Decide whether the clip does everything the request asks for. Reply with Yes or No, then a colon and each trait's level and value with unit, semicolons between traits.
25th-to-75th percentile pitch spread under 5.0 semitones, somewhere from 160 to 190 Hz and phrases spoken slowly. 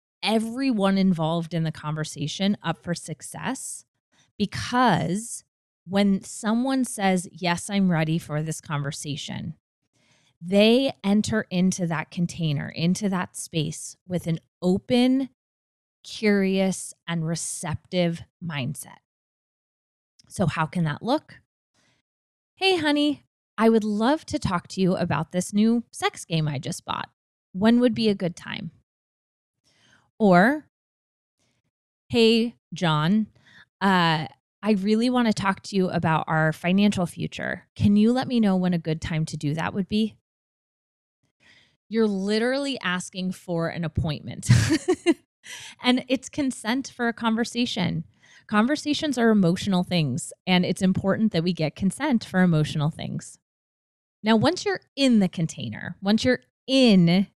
No: wide, 5.5 semitones; medium, 185 Hz; slow, 130 wpm